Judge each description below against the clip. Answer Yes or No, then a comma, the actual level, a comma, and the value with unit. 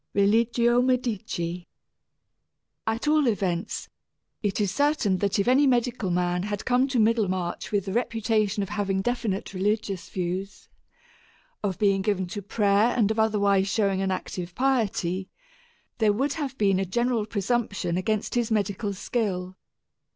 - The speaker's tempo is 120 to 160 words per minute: Yes, average, 145 wpm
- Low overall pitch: No, high, 205 Hz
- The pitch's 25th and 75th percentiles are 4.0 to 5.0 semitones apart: No, average, 3.5 semitones